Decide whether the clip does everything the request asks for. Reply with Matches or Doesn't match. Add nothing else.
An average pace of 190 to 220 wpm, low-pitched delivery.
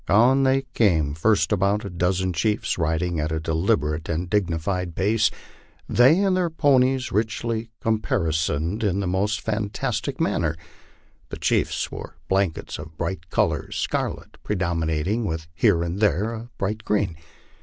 Doesn't match